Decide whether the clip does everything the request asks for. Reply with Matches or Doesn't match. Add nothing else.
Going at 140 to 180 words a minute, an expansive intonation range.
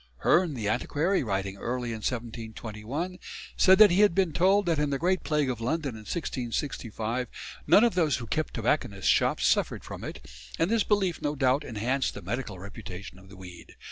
Doesn't match